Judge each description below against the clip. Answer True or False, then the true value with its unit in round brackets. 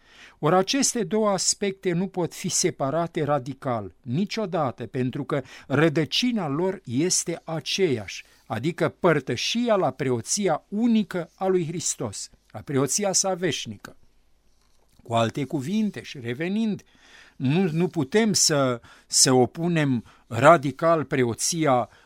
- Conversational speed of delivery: False (110 wpm)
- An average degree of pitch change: False (6.4 semitones)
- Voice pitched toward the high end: False (165 Hz)